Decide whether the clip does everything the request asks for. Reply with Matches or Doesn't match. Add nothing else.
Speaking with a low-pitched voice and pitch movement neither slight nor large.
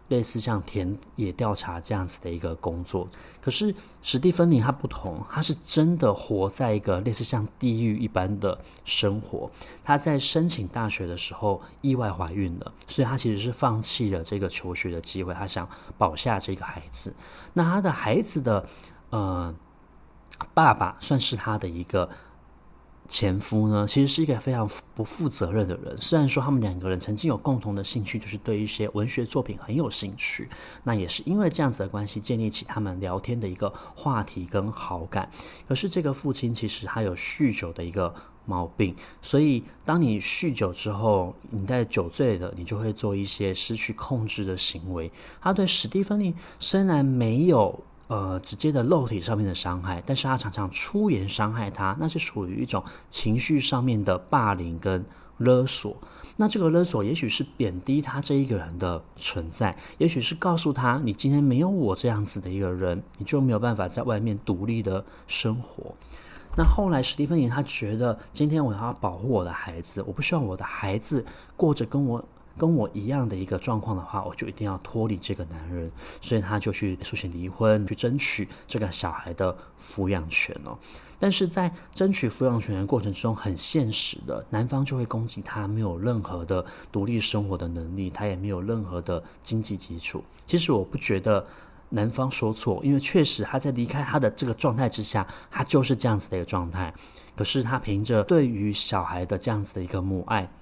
Doesn't match